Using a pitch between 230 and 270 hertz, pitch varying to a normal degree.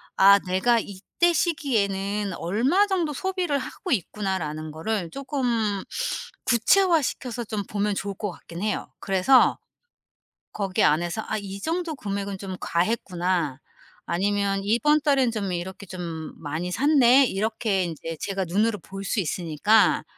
No: high, 200 Hz; average, 4.9 semitones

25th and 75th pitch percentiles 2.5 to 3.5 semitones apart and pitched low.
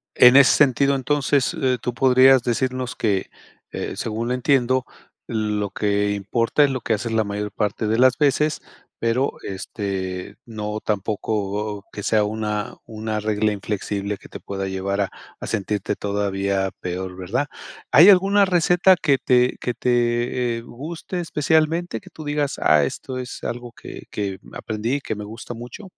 No: average, 4.3 semitones; low, 115 Hz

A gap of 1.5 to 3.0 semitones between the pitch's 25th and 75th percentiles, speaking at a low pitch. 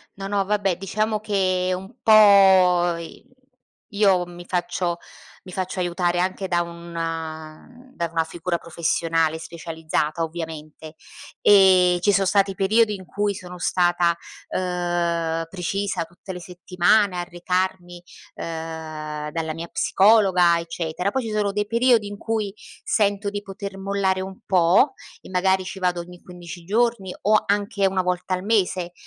No: narrow, 2.6 semitones; medium, 180 Hz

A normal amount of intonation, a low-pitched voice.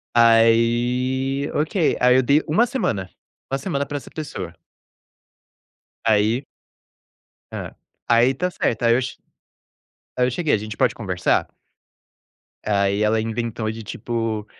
Yes: average, 3.6 semitones; low, 120 Hz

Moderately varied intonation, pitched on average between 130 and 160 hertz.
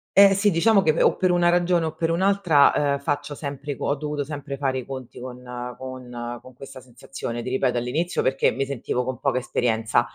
Yes: average, 4.3 semitones; medium, 140 Hz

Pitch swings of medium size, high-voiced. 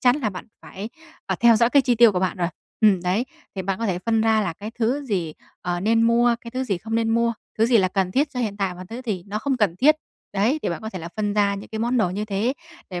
Yes: average, 3.7 semitones; high, 215 Hz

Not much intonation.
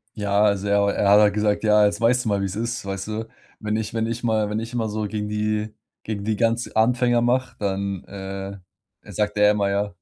Yes: narrow, 1.7 semitones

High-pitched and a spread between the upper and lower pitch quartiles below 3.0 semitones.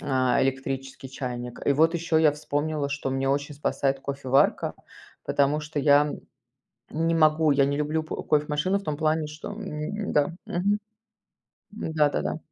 No: medium, 150 Hz; narrow, 2.4 semitones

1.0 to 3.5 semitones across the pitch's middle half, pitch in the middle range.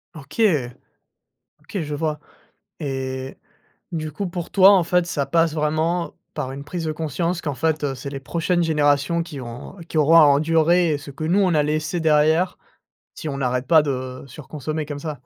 Yes: average, 2.8 semitones; medium, 155 Hz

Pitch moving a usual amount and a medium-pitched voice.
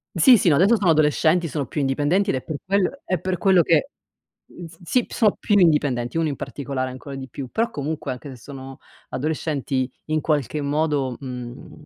Yes: average, 4.5 semitones; medium, 150 Hz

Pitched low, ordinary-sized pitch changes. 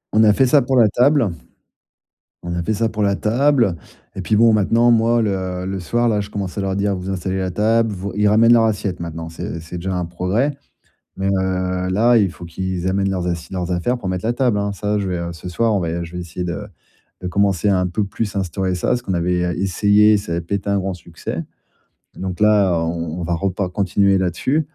Yes: very low, 95 Hz; average, 3.0 semitones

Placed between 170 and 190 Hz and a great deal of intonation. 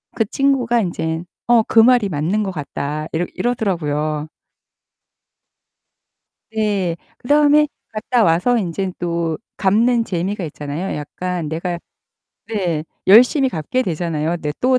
Yes: medium, 185 Hz; wide, 6.1 semitones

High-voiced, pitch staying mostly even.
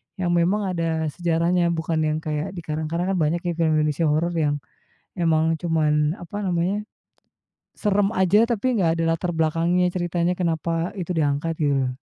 No: medium, 170 Hz; narrow, 2.2 semitones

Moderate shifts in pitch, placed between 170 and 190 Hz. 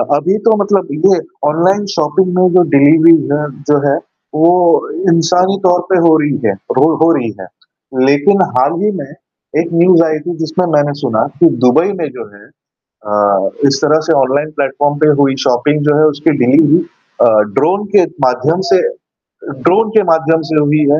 No: average, 3.7 semitones; medium, 160 Hz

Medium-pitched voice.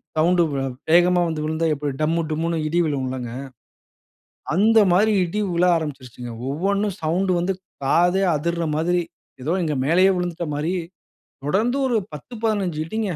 Yes: medium, 170 Hz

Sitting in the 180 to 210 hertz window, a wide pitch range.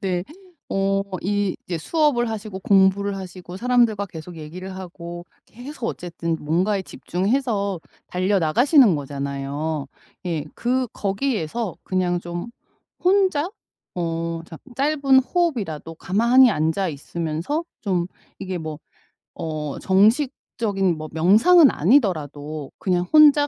Yes: high, 190 Hz; wide, 6.2 semitones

